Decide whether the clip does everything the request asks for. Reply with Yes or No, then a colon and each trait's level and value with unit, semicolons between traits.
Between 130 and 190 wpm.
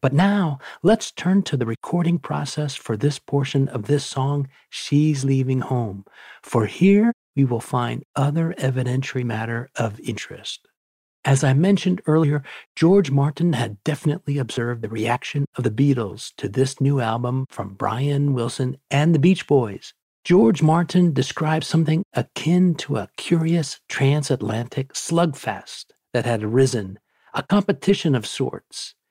Yes: average, 140 wpm